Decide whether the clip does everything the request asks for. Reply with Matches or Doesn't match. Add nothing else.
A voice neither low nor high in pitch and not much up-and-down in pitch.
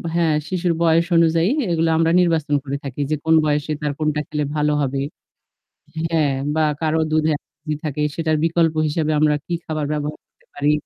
Matches